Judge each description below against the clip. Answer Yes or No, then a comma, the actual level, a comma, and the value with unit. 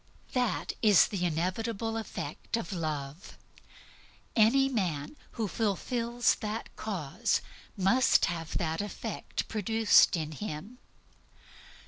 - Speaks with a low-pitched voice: No, high, 205 Hz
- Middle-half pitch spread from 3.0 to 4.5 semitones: No, average, 5.2 semitones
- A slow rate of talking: Yes, slow, 100 wpm